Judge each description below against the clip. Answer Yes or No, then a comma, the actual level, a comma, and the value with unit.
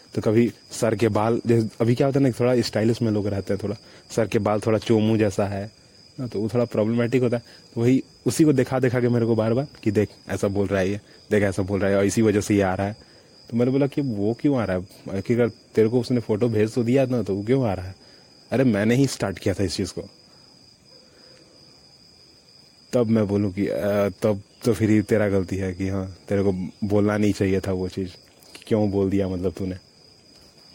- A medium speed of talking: No, fast, 240 wpm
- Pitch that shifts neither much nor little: Yes, average, 3.3 semitones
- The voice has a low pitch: Yes, low, 105 Hz